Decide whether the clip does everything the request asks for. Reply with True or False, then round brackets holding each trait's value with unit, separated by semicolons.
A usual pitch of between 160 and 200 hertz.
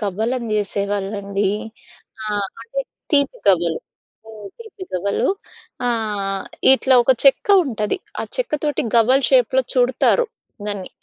False (220 Hz)